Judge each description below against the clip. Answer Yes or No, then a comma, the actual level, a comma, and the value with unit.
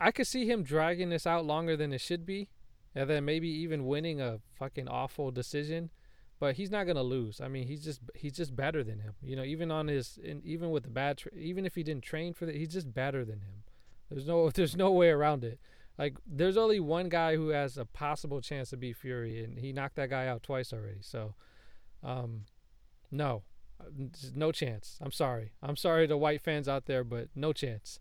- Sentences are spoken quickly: Yes, fast, 225 wpm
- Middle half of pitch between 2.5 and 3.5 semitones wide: No, average, 4.1 semitones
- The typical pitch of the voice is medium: Yes, medium, 145 Hz